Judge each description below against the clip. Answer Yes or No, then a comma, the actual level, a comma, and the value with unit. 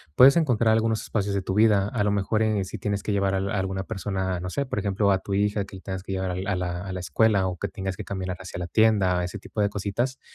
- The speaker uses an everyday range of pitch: No, narrow, 2.0 semitones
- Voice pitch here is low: Yes, low, 100 Hz